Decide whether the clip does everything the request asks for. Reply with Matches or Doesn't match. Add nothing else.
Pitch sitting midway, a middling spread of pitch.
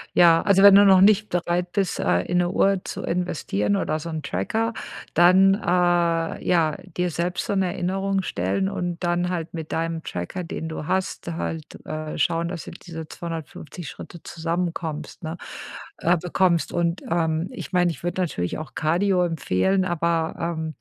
Doesn't match